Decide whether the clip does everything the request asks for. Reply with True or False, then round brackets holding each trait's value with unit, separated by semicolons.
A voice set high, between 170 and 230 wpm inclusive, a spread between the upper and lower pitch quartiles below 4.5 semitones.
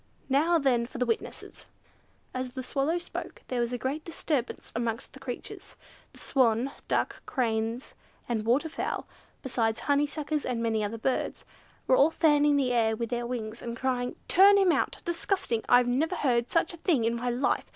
True (255 Hz; 180 wpm; 3.9 semitones)